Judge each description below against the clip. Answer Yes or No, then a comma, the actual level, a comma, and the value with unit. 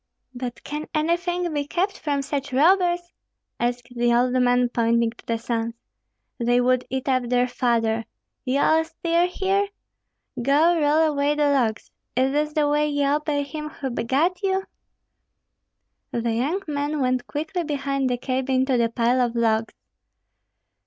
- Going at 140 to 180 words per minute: Yes, average, 155 wpm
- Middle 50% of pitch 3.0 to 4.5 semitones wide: Yes, average, 3.9 semitones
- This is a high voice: Yes, very high, 275 Hz